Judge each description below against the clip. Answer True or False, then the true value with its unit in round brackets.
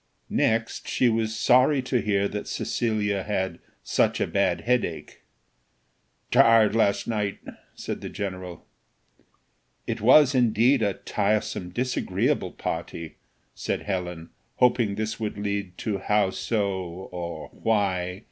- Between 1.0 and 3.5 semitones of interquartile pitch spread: True (3.1 semitones)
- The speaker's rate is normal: False (120 wpm)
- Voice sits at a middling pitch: False (105 Hz)